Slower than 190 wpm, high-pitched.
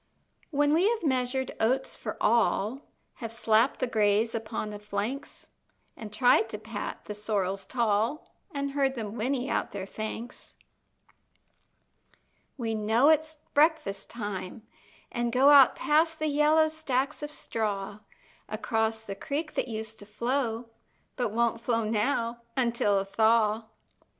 Yes: average, 140 wpm; high, 230 Hz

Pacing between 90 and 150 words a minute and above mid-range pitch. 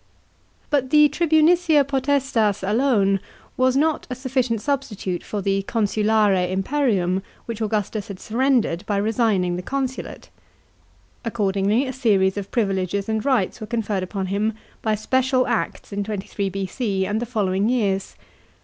Yes: average, 140 wpm; high, 215 Hz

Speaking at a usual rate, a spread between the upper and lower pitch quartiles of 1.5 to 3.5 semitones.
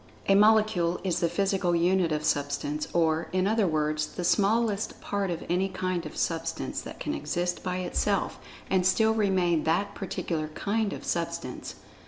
Yes: average, 165 wpm; average, 3.2 semitones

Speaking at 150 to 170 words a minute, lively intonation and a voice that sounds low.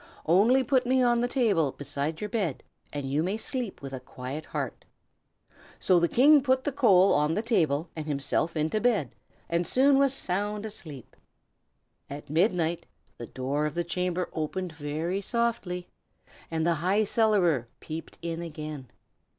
No: average, 165 wpm; wide, 6.3 semitones; medium, 175 Hz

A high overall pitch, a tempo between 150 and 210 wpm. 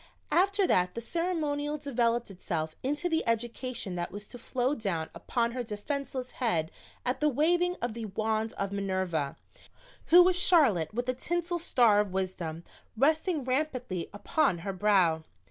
Yes: high, 240 Hz; average, 155 wpm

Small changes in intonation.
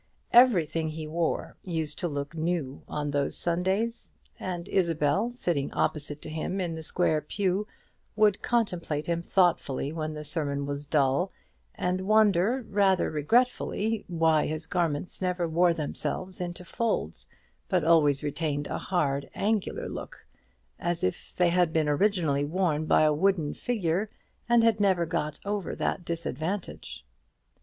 No: average, 3.8 semitones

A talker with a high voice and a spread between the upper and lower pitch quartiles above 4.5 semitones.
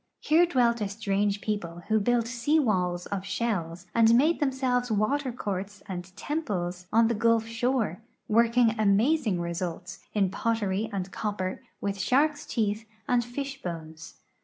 No: high, 215 Hz; average, 4.2 semitones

